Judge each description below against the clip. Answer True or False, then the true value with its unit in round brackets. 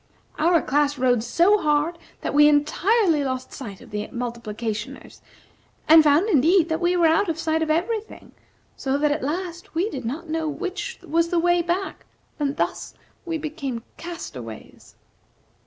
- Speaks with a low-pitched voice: False (315 Hz)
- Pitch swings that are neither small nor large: True (4.0 semitones)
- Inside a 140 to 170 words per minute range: True (165 wpm)